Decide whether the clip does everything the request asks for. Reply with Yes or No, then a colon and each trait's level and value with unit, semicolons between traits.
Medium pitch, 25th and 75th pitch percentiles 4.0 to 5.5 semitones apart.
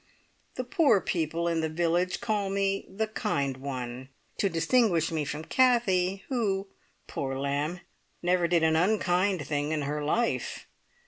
Yes: medium, 175 Hz; average, 4.8 semitones